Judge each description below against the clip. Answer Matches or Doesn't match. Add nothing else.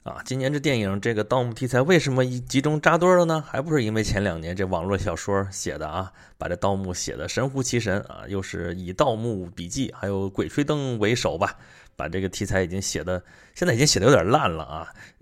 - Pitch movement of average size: Doesn't match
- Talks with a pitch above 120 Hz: Doesn't match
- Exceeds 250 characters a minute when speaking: Matches